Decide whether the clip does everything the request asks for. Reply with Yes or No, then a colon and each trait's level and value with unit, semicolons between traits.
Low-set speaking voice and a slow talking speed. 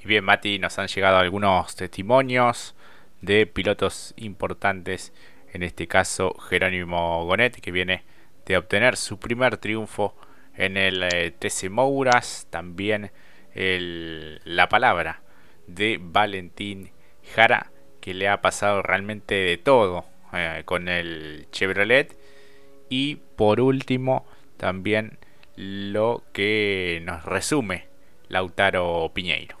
Yes: very low, 95 Hz; slow, 110 wpm